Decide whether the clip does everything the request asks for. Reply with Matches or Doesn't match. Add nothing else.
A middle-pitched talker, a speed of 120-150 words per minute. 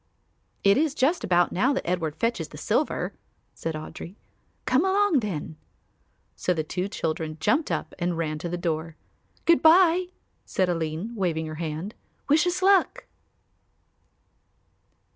Matches